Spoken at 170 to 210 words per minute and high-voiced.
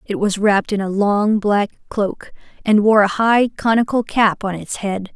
Yes: average, 200 wpm; high, 210 Hz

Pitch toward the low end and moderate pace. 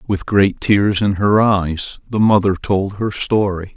Yes: low, 100 Hz; average, 175 wpm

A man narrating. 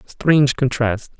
Yes: male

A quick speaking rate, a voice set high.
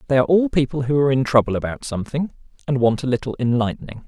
No: fast, 220 wpm; low, 130 Hz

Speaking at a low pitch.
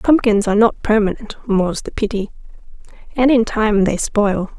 No: high, 215 Hz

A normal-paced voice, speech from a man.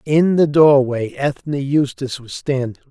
Yes: average, 145 wpm; male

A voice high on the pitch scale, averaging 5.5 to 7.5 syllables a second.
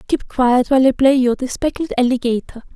Yes: very high, 255 Hz; 5.6 syllables/s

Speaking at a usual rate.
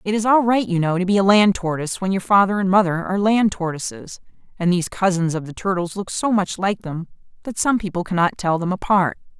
No: fast, 235 wpm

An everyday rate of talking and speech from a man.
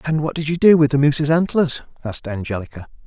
No: fast, 215 wpm; male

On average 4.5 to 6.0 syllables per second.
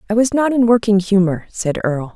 Yes: 5.9 syllables/s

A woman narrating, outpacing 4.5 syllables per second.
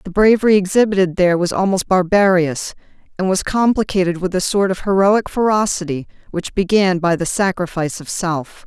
Yes: female; 5.5 syllables/s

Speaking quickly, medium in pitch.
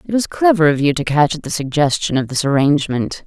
Yes: fast, 240 wpm; medium, 155 Hz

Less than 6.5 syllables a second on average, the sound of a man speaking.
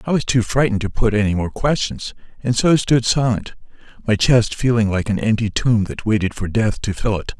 Yes: 5.4 syllables/s; male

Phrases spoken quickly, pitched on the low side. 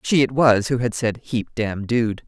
Yes: fast, 235 wpm; low, 115 Hz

